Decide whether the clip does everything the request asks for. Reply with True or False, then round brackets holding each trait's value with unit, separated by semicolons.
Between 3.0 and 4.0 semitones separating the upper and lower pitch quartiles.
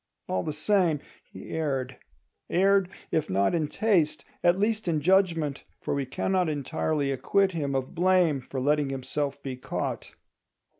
False (4.9 semitones)